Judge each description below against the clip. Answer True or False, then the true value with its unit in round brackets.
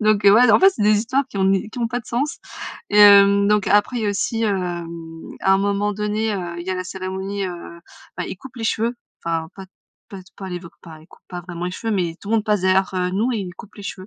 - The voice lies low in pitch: False (200 Hz)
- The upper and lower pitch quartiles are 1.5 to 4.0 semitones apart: True (2.7 semitones)